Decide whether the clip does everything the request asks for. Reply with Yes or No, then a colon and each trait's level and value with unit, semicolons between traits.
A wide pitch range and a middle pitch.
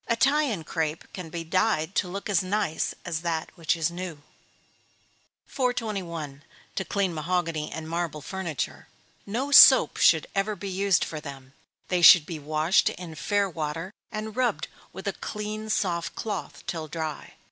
No: average, 4.2 semitones; medium, 175 Hz